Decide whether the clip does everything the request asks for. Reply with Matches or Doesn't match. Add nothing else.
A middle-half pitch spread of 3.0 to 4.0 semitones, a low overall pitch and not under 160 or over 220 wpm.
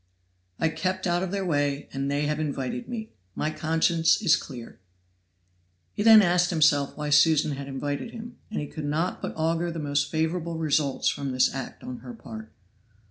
Doesn't match